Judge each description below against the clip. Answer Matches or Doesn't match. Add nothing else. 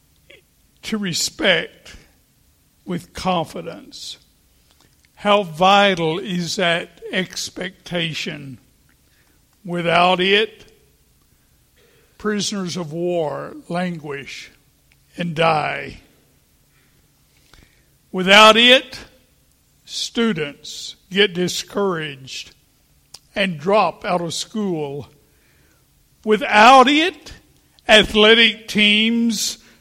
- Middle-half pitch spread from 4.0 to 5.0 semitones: Matches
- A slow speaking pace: Matches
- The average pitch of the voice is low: Doesn't match